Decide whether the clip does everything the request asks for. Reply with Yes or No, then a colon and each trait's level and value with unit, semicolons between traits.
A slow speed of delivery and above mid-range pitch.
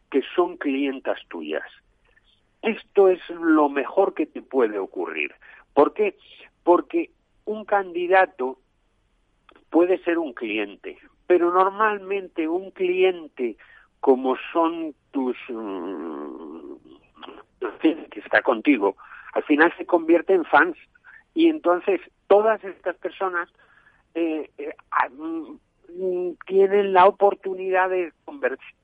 Yes: slow, 100 wpm; high, 195 Hz